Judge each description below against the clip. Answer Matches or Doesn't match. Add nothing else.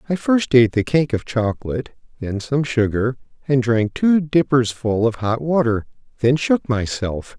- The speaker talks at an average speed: Matches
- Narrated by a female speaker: Doesn't match